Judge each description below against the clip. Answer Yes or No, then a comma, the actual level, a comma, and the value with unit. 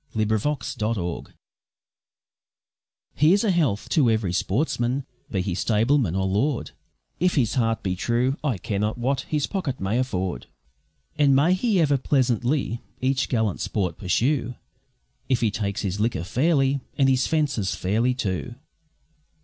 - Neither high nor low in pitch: No, low, 120 Hz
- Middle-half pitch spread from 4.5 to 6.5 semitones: Yes, average, 5.1 semitones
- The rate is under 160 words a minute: Yes, average, 145 wpm